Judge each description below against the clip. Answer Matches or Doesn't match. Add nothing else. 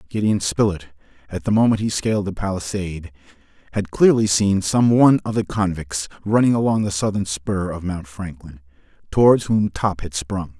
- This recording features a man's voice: Matches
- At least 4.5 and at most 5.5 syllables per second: Matches